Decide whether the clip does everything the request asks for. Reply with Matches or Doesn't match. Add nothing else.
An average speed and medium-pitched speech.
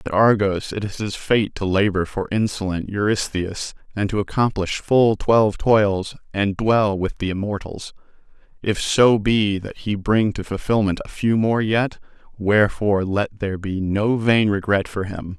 Doesn't match